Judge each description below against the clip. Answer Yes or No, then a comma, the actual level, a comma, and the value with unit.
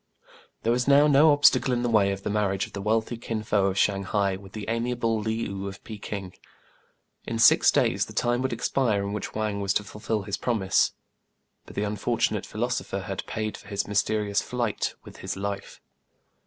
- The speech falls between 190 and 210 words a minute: Yes, average, 200 wpm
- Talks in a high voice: No, low, 105 Hz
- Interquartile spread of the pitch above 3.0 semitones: No, narrow, 2.6 semitones